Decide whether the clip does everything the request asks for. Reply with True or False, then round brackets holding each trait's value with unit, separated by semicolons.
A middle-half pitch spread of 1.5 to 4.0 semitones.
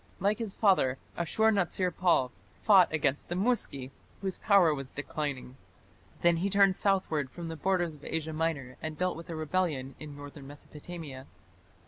False (4.5 semitones)